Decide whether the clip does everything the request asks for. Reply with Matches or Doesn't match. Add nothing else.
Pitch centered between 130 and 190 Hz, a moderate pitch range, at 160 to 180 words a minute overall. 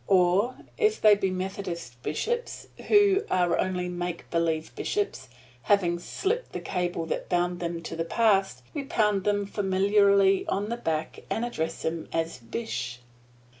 Doesn't match